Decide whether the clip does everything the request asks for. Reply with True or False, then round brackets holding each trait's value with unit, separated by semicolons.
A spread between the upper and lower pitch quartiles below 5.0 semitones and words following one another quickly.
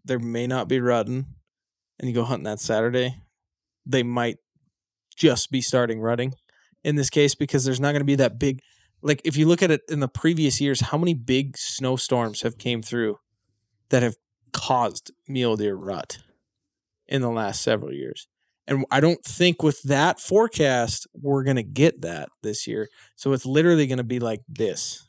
False (3.3 semitones; 185 wpm)